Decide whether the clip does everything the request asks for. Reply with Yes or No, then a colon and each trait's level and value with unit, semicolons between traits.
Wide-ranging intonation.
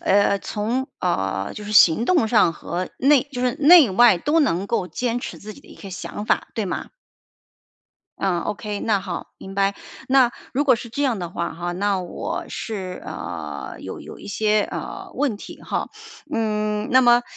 No: average, 4.3 semitones